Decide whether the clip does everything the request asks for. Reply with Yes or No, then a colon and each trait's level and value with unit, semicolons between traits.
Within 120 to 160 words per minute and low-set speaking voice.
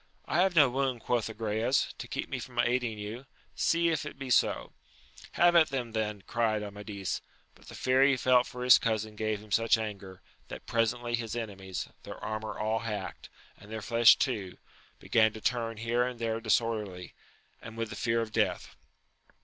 No: average, 190 wpm; low, 115 Hz